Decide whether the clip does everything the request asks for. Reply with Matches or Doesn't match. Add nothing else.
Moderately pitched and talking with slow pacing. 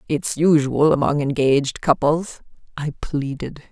Matches